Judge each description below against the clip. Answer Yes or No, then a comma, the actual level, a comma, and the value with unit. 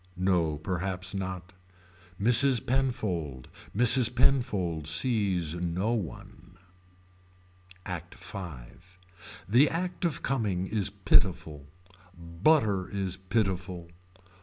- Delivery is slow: Yes, slow, 85 wpm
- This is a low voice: Yes, very low, 95 Hz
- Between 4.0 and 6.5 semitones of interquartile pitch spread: Yes, average, 4.7 semitones